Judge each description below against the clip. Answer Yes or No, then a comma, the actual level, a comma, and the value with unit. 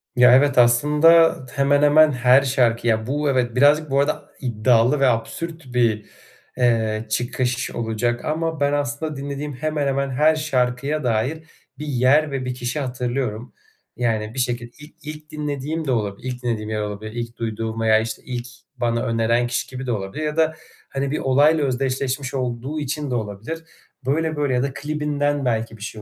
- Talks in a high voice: No, low, 130 Hz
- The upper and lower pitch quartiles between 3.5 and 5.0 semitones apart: Yes, average, 3.8 semitones